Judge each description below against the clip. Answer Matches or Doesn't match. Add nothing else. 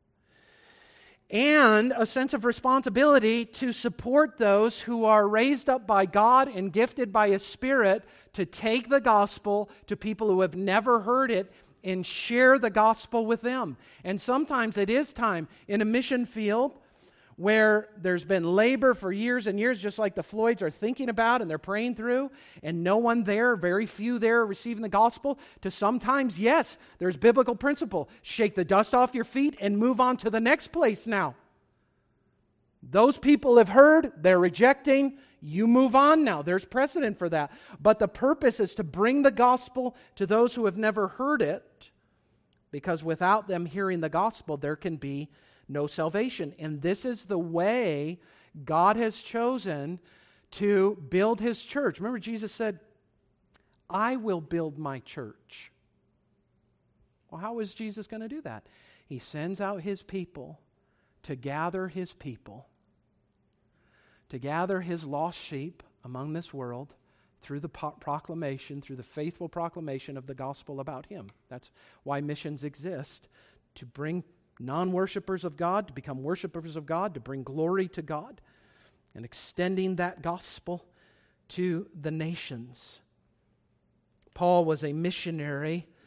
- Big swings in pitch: Matches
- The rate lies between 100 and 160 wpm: Matches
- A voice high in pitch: Matches